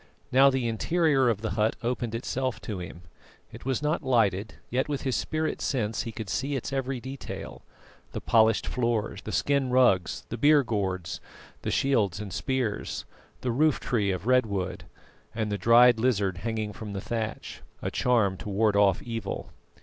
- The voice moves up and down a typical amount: Yes, average, 4.1 semitones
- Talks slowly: No, average, 175 wpm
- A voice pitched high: No, low, 115 Hz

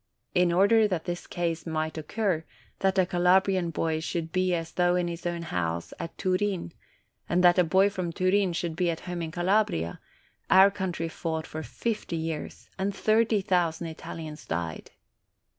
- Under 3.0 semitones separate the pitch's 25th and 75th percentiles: Yes, narrow, 2.6 semitones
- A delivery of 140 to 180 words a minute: Yes, average, 170 wpm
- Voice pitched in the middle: Yes, medium, 175 Hz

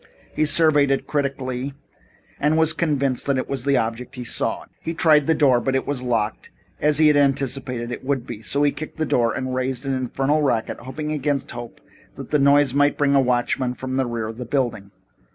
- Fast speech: Yes, fast, 215 wpm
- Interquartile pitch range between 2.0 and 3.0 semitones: Yes, narrow, 2.6 semitones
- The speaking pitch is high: No, low, 135 Hz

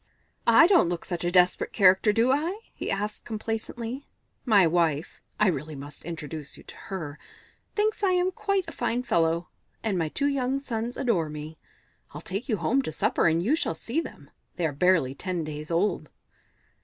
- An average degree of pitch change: No, wide, 7.5 semitones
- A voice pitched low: No, high, 190 Hz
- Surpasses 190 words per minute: No, average, 185 wpm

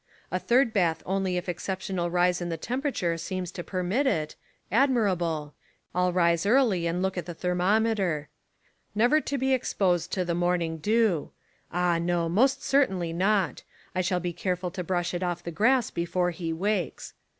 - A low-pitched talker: No, medium, 180 Hz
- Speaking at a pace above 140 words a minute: Yes, average, 175 wpm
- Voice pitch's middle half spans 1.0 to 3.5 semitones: Yes, average, 3.2 semitones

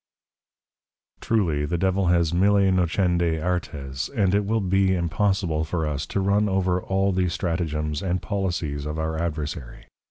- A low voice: Yes, very low, 90 Hz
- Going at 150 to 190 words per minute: Yes, average, 155 wpm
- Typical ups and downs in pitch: Yes, average, 3.5 semitones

